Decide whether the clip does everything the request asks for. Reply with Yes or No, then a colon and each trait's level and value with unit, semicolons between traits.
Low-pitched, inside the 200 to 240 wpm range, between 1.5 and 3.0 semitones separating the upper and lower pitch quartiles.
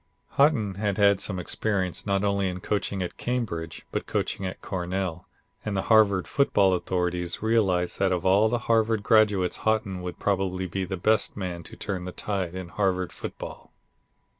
No: very low, 95 Hz; average, 170 wpm; narrow, 2.5 semitones